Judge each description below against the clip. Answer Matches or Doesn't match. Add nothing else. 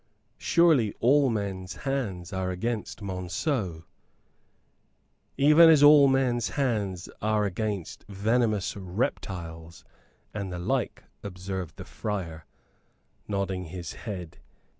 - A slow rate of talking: Matches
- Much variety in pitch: Doesn't match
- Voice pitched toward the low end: Matches